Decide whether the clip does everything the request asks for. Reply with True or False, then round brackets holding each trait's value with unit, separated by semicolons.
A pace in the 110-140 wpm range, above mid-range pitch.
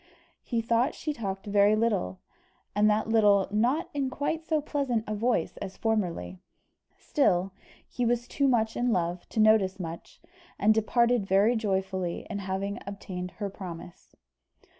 False (150 wpm; 215 Hz)